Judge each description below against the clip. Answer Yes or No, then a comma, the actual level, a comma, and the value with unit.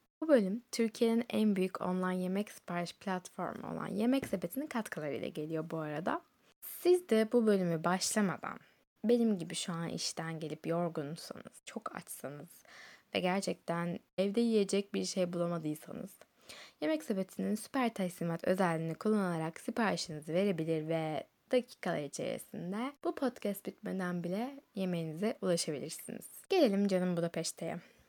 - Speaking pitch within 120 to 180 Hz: No, high, 190 Hz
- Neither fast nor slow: Yes, average, 120 wpm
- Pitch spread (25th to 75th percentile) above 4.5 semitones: Yes, average, 5.0 semitones